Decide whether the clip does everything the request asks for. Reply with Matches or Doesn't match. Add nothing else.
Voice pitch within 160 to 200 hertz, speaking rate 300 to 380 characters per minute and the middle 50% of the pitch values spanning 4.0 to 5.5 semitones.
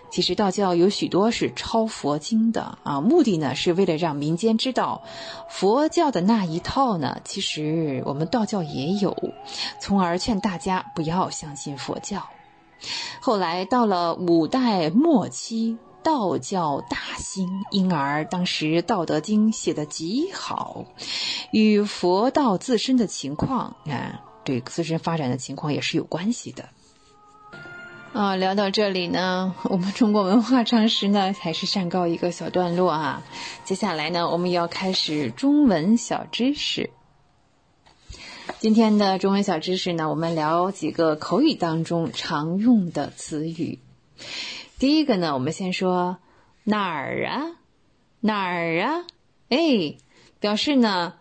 Doesn't match